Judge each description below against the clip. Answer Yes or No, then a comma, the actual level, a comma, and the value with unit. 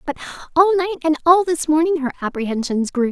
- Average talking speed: Yes, average, 190 wpm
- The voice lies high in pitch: Yes, very high, 305 Hz